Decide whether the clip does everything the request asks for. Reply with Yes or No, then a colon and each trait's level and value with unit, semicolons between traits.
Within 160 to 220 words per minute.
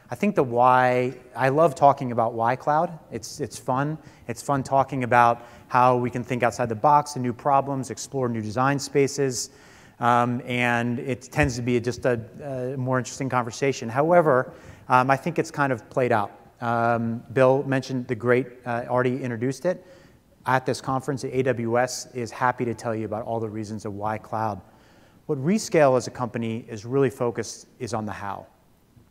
Yes: average, 185 wpm